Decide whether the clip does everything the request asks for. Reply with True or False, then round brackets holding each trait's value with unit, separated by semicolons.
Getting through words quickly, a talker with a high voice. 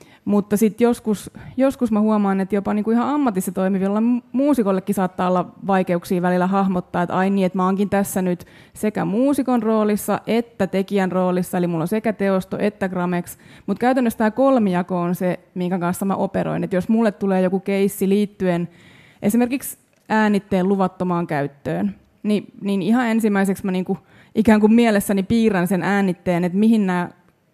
True (170 wpm; 195 Hz)